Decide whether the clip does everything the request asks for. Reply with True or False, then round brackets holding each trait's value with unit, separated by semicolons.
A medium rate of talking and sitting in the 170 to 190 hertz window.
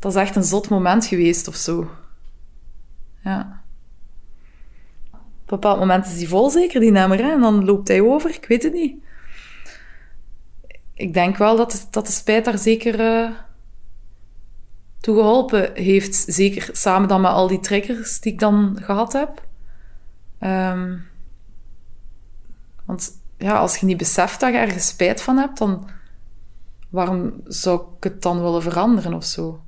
True (160 wpm; 185 Hz)